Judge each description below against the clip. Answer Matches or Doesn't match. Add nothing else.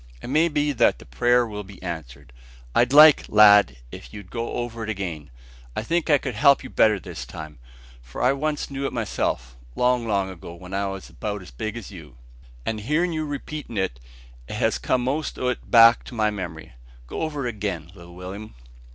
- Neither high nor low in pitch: Doesn't match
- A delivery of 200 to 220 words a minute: Matches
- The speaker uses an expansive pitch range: Matches